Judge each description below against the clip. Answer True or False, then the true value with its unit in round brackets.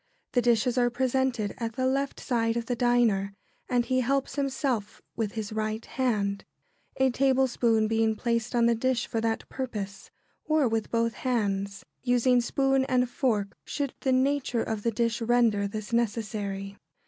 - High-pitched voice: True (235 Hz)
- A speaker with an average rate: True (160 wpm)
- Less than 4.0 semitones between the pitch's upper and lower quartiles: True (3.0 semitones)